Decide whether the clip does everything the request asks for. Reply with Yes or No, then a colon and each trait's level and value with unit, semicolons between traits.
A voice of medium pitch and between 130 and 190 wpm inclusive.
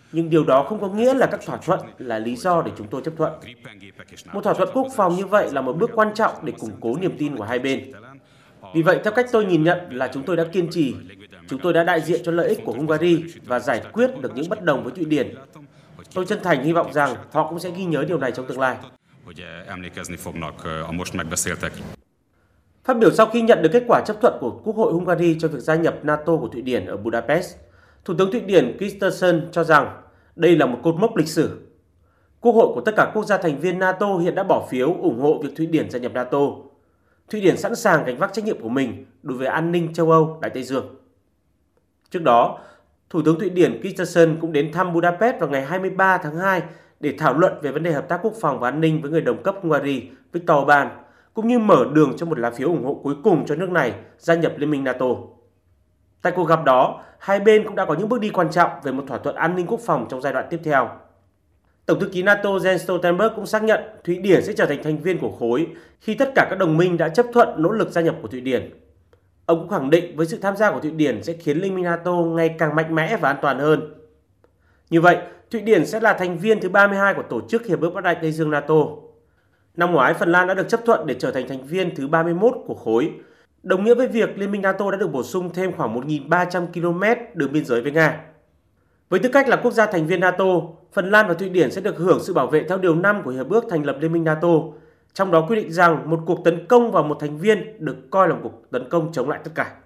No: medium, 165 Hz; fast, 250 wpm